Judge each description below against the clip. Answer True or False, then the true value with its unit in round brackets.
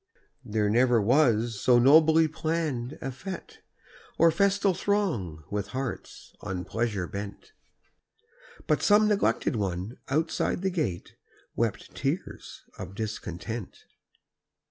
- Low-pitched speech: True (120 Hz)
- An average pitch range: False (7.8 semitones)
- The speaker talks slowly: True (110 wpm)